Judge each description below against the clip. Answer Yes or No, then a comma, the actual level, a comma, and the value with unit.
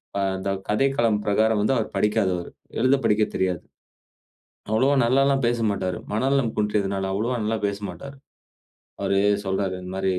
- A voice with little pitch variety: No, average, 3.7 semitones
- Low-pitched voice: Yes, low, 105 Hz